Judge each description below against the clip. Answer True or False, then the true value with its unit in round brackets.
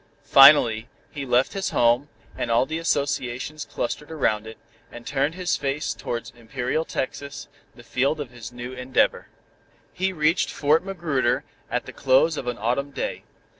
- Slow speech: False (160 wpm)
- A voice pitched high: False (135 Hz)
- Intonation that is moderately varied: True (3.9 semitones)